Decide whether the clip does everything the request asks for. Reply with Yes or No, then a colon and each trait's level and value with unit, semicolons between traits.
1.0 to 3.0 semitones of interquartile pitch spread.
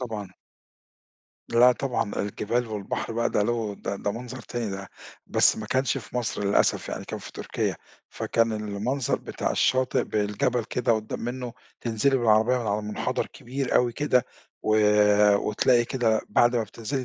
Yes: average, 2.7 semitones